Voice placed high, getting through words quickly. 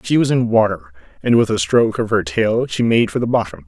No: low, 110 Hz; fast, 260 wpm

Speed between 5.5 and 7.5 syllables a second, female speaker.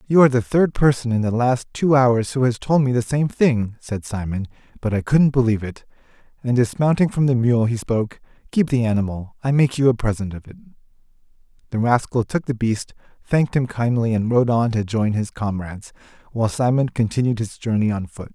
No: 5.6 syllables/s; male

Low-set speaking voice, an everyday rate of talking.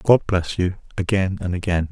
Yes: very low, 95 Hz; average, 190 wpm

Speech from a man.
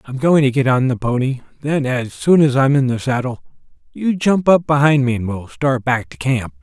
Yes: male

